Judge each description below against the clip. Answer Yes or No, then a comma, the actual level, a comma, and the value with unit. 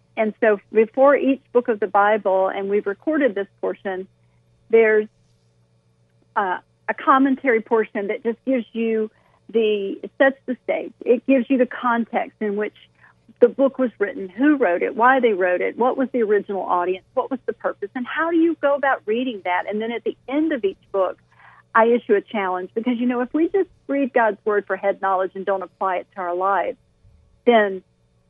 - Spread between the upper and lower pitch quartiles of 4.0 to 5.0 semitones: Yes, average, 4.5 semitones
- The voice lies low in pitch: No, high, 225 Hz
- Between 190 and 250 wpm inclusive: Yes, average, 200 wpm